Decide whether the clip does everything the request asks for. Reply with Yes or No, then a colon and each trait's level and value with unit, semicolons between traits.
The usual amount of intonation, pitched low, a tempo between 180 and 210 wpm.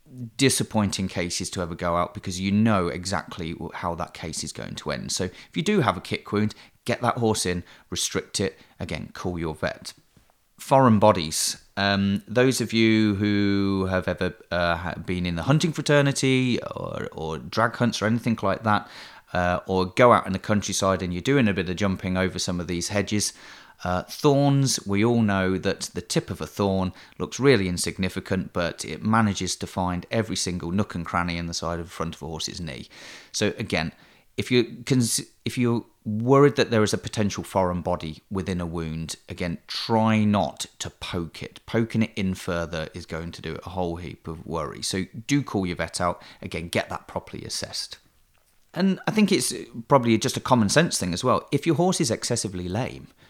Yes: average, 4.5 semitones; low, 100 Hz; average, 200 wpm